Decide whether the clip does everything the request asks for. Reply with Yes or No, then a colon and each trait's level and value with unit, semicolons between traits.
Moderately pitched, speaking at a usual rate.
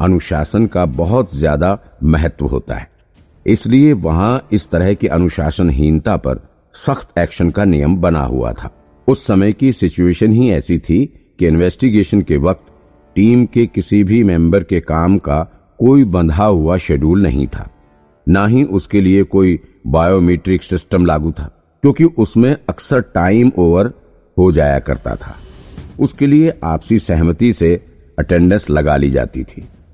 No: very low, 90 Hz; average, 150 wpm